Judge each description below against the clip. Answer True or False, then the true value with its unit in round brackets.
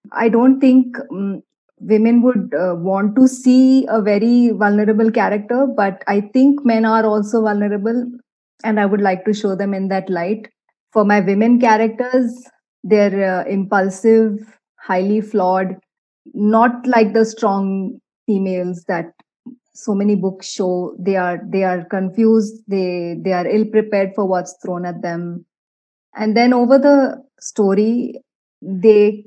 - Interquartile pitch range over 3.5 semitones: False (3.2 semitones)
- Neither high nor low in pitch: False (210 Hz)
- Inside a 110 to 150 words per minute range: True (145 wpm)